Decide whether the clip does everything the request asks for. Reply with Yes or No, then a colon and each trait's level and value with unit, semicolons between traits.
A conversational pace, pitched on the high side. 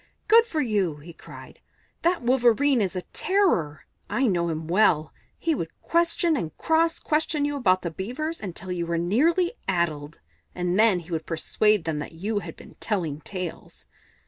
Yes: average, 170 wpm; high, 195 Hz